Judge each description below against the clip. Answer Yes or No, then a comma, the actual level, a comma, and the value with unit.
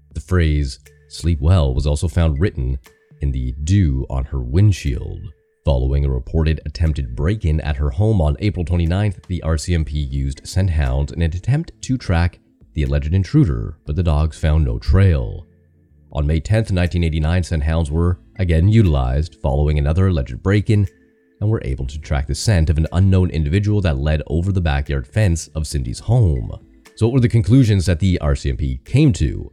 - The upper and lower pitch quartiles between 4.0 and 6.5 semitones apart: Yes, average, 4.3 semitones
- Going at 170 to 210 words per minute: Yes, average, 180 wpm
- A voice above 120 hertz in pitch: No, very low, 80 Hz